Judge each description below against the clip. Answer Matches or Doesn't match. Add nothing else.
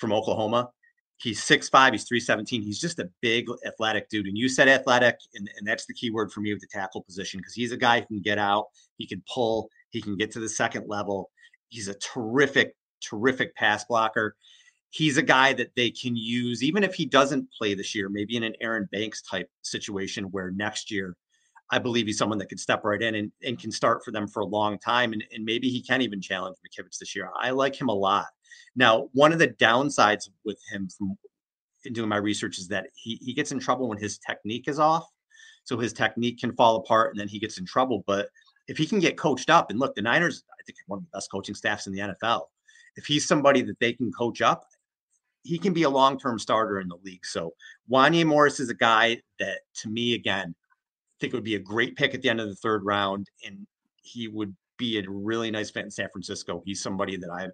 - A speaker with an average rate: Doesn't match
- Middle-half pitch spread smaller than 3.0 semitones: Doesn't match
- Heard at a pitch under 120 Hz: Matches